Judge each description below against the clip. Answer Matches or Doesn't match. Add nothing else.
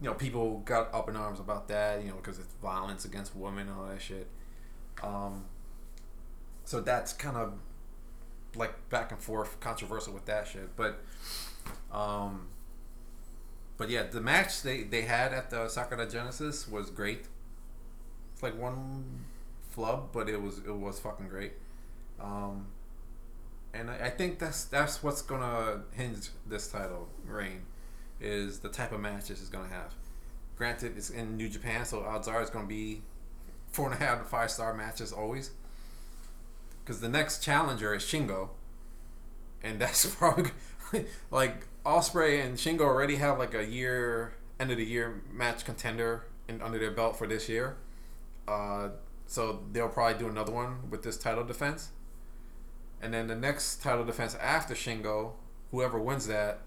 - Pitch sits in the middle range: Doesn't match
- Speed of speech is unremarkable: Matches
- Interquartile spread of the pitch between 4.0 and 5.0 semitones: Doesn't match